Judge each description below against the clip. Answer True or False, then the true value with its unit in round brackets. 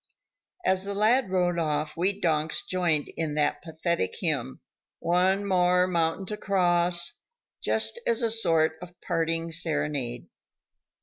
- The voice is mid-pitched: True (175 Hz)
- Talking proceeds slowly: True (130 wpm)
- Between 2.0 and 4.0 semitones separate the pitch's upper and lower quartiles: True (2.9 semitones)